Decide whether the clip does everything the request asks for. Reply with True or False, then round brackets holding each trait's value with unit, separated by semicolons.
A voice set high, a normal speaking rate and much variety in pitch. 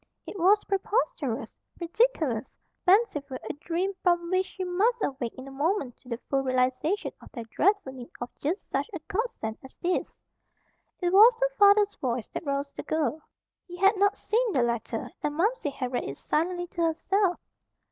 True (345 Hz; 175 wpm; 6.9 semitones)